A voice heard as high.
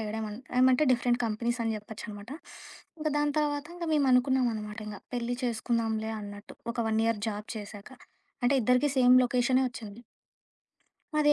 Yes: high, 235 Hz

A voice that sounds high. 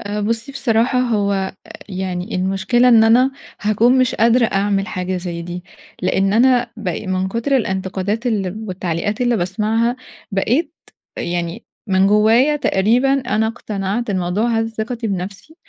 Yes: high, 210 Hz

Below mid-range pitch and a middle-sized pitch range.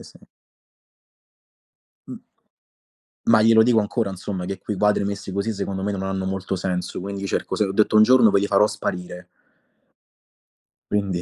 No: low, 100 Hz; narrow, 1.8 semitones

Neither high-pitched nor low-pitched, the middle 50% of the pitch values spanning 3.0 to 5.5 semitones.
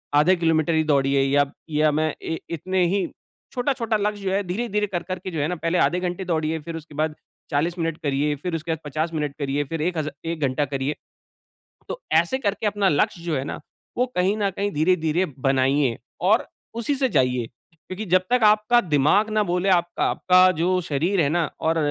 Yes: medium, 170 Hz; average, 4.2 semitones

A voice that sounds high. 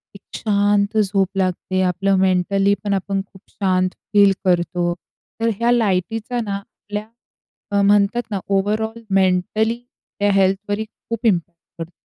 Yes: high, 200 Hz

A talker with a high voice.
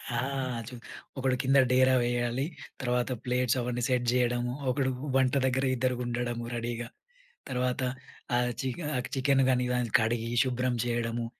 No: low, 125 Hz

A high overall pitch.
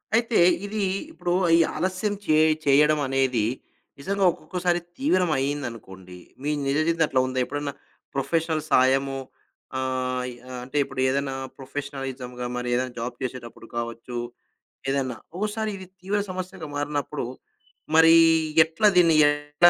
No: medium, 145 Hz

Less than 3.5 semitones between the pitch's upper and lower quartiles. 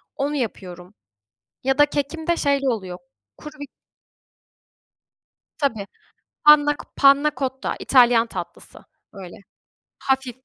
No: average, 4.4 semitones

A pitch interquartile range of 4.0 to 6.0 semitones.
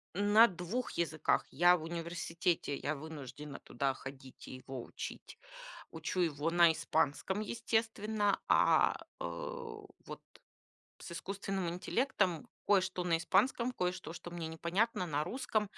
Yes: average, 4.5 semitones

